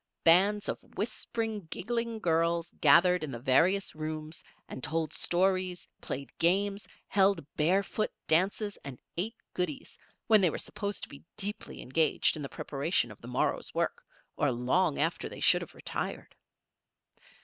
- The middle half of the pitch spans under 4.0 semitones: No, average, 4.4 semitones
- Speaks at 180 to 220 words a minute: No, average, 150 wpm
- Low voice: No, medium, 175 Hz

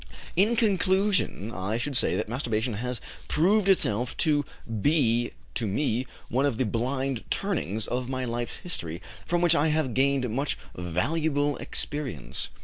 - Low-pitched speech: Yes, low, 130 Hz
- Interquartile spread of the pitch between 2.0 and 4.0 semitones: No, average, 5.2 semitones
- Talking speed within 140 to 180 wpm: Yes, average, 145 wpm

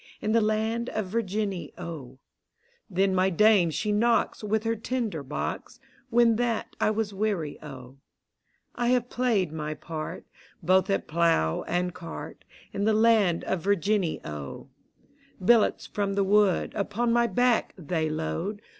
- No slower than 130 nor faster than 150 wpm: Yes, average, 145 wpm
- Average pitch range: Yes, average, 4.8 semitones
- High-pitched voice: Yes, high, 200 Hz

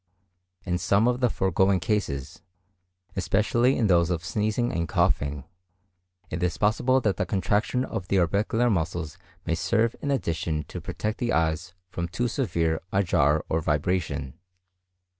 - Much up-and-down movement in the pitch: No, average, 4.8 semitones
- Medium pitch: No, very low, 95 Hz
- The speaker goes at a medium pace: Yes, average, 150 wpm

